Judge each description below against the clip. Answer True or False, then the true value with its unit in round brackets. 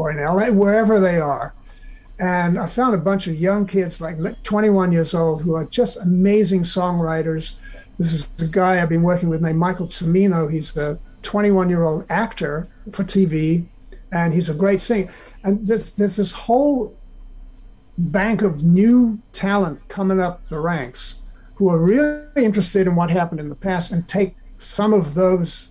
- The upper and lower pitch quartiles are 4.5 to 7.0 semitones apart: False (3.6 semitones)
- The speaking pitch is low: False (180 Hz)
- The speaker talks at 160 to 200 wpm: True (175 wpm)